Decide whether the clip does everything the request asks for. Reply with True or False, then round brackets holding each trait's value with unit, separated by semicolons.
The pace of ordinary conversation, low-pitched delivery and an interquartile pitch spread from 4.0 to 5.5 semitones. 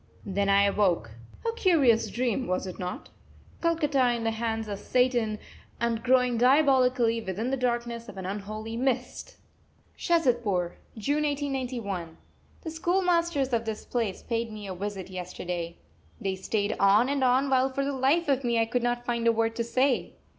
False (170 wpm; 235 Hz; 4.3 semitones)